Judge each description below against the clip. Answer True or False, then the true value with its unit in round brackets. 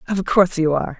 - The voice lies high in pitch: False (170 Hz)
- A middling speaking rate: False (240 wpm)